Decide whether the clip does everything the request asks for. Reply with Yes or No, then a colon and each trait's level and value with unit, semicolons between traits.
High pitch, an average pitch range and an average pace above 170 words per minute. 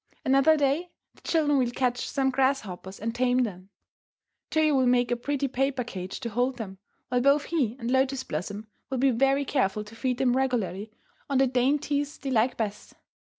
Yes: very high, 255 Hz; average, 3.0 semitones; average, 185 wpm